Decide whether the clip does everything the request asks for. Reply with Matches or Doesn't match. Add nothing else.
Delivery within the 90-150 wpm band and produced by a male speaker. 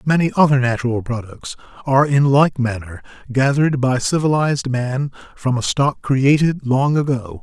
Matches